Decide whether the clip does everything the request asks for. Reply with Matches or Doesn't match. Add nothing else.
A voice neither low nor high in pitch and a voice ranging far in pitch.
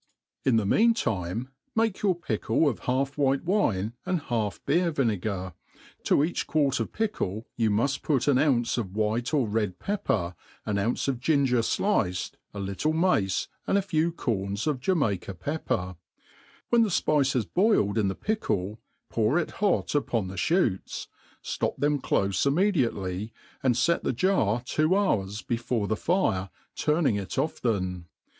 Doesn't match